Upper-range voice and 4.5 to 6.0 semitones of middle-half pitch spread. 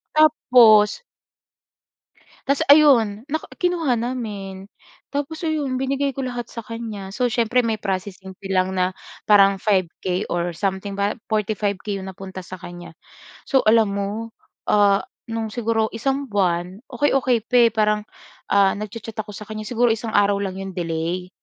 No: high, 210 Hz; average, 4.0 semitones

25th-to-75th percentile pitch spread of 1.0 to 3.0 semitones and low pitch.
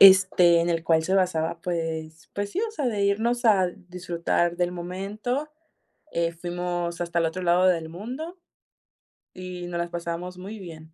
No: narrow, 2.5 semitones; medium, 180 Hz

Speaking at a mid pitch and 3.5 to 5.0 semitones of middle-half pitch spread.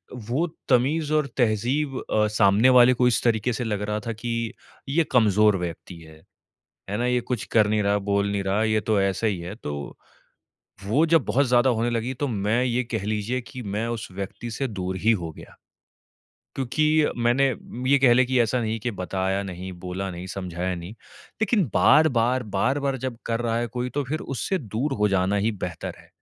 No: low, 115 Hz; average, 4.1 semitones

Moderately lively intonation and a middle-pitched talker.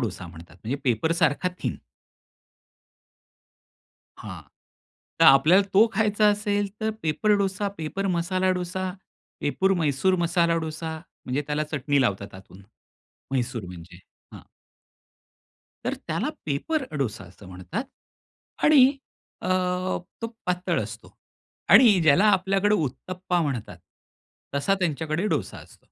No: wide, 6.3 semitones; medium, 165 Hz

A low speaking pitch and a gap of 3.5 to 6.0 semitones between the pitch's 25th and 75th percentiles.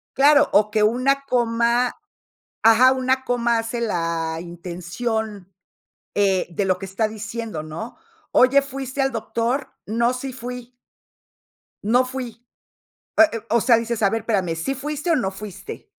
No: high, 230 Hz; average, 3.9 semitones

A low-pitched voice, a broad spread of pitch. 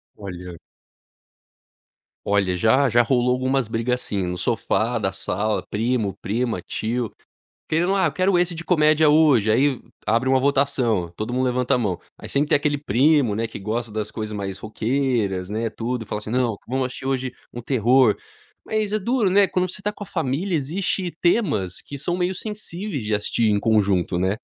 Yes: low, 125 Hz; wide, 6.0 semitones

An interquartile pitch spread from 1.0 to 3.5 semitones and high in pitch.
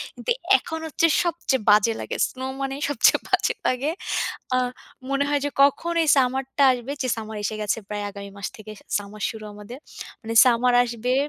No: average, 4.3 semitones; very high, 250 Hz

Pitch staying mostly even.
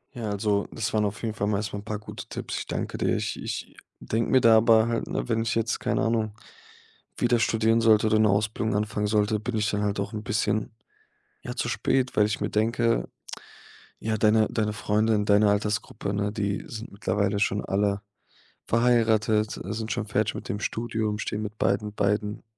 Yes: narrow, 1.4 semitones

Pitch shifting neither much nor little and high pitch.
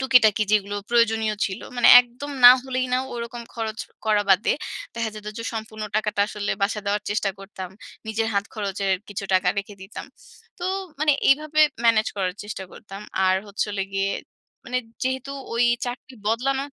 Yes: average, 3.3 semitones; high, 220 Hz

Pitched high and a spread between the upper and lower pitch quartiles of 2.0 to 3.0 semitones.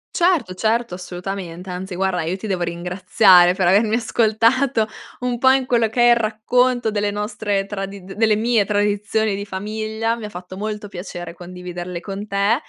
No: high, 205 Hz; average, 3.4 semitones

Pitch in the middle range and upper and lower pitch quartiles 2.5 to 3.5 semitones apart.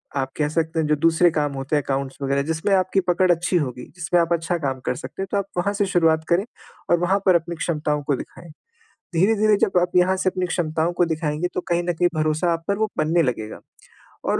Yes: medium, 170 Hz; average, 2.8 semitones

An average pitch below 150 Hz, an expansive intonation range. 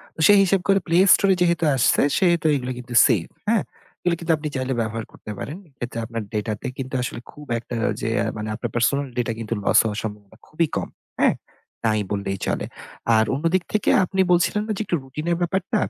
Yes: low, 135 Hz; wide, 7.5 semitones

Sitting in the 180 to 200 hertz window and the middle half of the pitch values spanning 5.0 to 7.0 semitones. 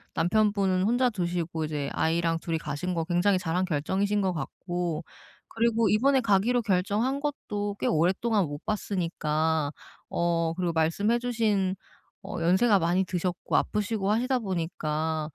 No: medium, 185 Hz; average, 4.3 semitones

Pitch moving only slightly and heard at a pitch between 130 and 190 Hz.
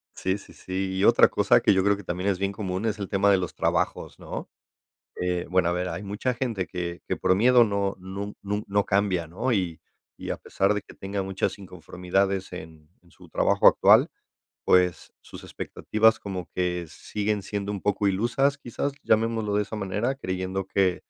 No: narrow, 2.1 semitones; very low, 95 Hz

